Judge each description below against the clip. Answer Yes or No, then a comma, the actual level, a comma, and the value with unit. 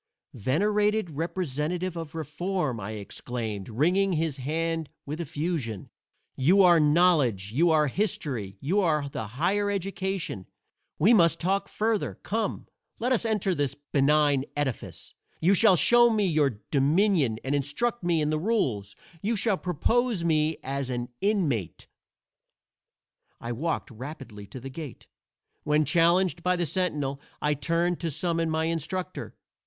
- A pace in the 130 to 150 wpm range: Yes, average, 140 wpm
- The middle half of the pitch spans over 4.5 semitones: Yes, average, 5.1 semitones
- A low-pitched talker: No, medium, 160 Hz